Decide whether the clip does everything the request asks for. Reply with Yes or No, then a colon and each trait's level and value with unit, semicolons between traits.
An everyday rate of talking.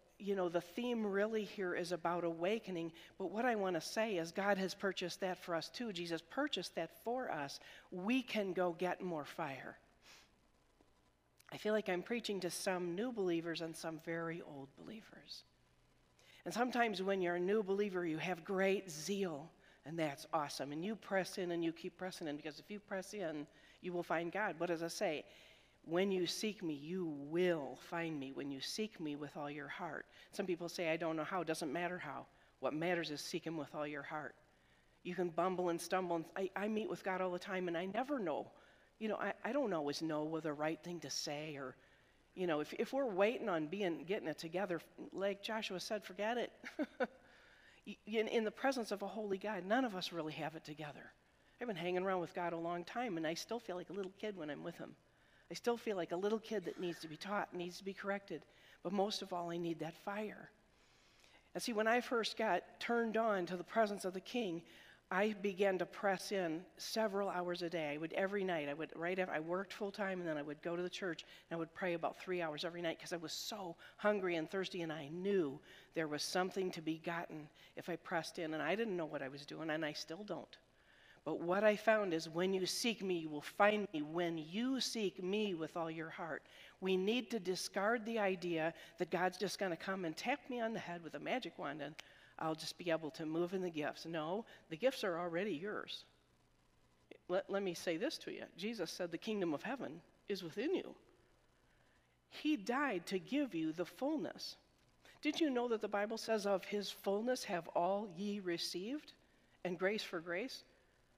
No: fast, 225 wpm